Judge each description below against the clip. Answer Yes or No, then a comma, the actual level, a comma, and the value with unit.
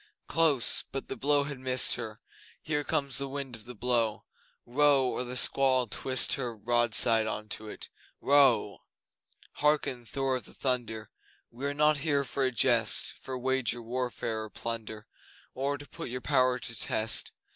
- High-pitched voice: No, low, 125 Hz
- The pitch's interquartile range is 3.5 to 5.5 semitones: No, average, 3.0 semitones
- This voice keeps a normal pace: Yes, average, 170 wpm